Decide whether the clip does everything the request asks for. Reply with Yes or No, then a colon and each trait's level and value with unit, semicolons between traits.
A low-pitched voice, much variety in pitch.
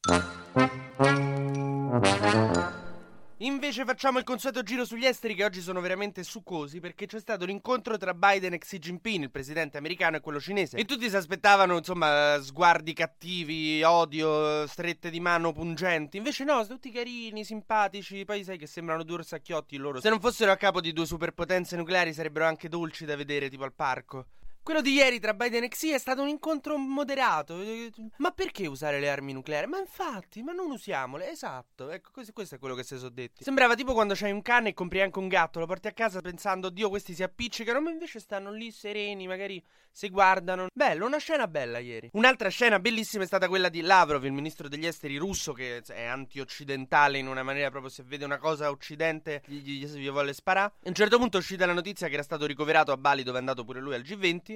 No: medium, 180 Hz; wide, 6.7 semitones